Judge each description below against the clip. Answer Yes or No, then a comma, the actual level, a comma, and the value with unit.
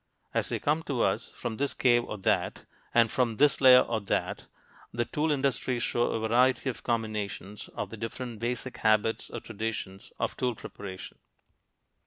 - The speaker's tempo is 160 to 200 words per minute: Yes, average, 170 wpm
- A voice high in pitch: No, low, 120 Hz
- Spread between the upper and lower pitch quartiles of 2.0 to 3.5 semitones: Yes, average, 2.8 semitones